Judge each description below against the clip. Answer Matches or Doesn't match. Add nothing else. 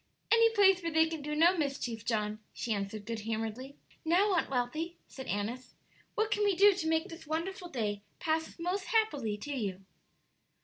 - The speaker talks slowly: Doesn't match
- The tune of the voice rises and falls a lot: Matches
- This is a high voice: Matches